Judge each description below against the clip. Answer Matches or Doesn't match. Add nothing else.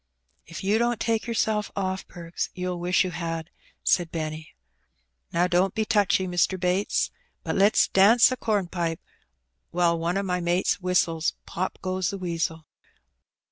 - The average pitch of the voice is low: Doesn't match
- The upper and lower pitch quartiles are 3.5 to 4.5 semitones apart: Doesn't match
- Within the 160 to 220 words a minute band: Doesn't match